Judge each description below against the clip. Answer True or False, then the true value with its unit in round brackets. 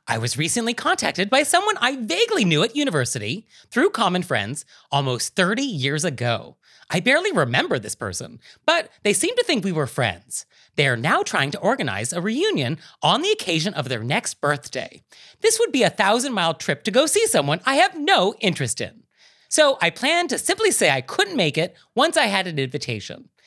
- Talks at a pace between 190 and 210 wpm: True (195 wpm)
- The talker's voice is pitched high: True (195 Hz)